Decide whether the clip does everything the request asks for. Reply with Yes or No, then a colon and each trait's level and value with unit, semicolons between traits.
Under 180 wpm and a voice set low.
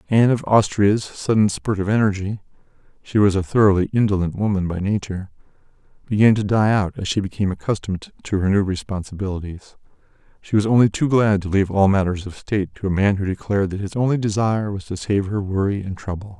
No: average, 190 wpm; low, 100 Hz